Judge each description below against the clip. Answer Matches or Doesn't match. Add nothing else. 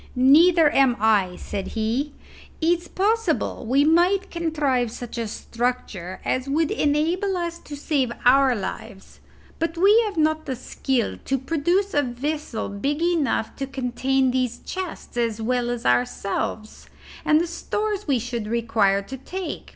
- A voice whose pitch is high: Matches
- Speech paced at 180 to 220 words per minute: Doesn't match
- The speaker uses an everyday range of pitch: Doesn't match